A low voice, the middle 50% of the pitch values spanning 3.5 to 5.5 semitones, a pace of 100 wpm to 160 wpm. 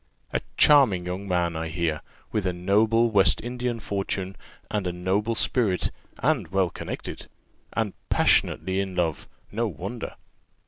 Yes: very low, 95 Hz; average, 4.0 semitones; average, 140 wpm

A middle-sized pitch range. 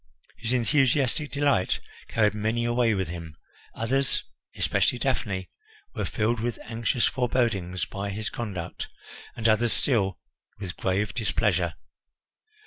Yes: average, 3.8 semitones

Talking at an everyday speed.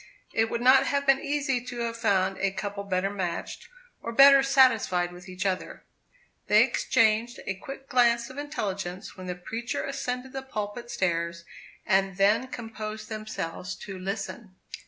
Yes: average, 155 wpm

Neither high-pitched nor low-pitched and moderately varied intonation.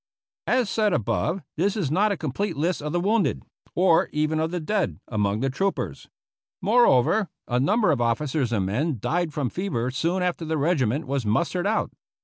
No: medium, 160 Hz; wide, 6.3 semitones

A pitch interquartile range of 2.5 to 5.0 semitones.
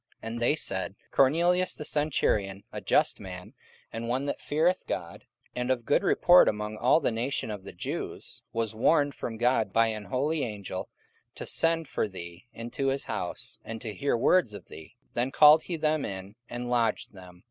No: wide, 5.6 semitones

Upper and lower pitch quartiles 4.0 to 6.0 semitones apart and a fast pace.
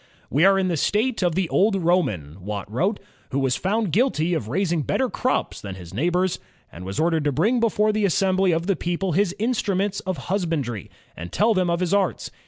Yes: average, 5.3 semitones; fast, 210 wpm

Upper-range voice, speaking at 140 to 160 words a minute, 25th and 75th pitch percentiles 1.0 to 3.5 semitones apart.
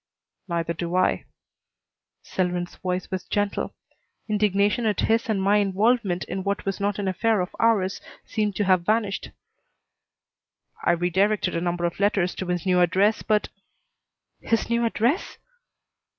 Yes: high, 195 Hz; average, 150 wpm; average, 2.8 semitones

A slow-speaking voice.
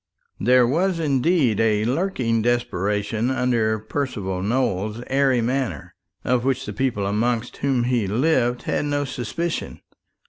Yes: slow, 130 wpm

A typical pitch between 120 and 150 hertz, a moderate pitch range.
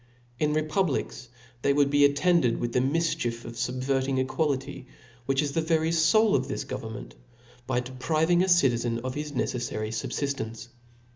Yes: low, 135 Hz; average, 4.1 semitones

